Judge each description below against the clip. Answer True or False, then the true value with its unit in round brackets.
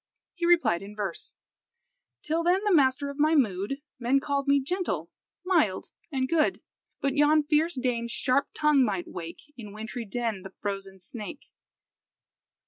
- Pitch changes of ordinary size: False (6.5 semitones)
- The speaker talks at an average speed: True (150 wpm)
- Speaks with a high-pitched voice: True (265 Hz)